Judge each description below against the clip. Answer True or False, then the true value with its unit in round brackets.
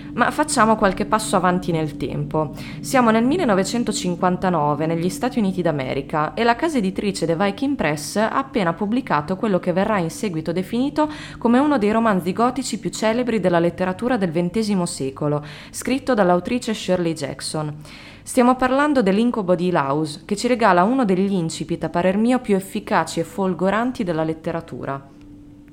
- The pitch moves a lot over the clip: True (6.0 semitones)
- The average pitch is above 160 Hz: True (190 Hz)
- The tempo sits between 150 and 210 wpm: True (155 wpm)